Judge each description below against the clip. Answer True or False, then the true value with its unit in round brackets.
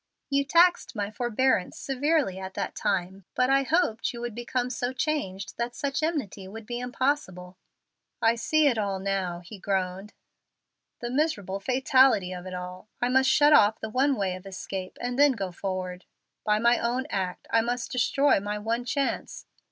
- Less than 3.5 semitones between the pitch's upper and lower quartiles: False (5.5 semitones)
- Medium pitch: False (230 Hz)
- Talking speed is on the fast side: False (175 wpm)